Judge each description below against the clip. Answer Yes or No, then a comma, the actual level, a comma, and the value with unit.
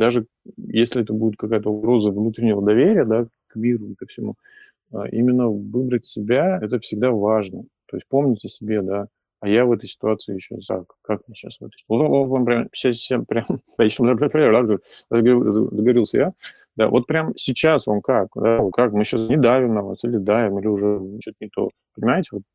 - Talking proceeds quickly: Yes, fast, 165 wpm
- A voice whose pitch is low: Yes, low, 115 Hz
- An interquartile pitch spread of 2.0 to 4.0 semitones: Yes, average, 2.7 semitones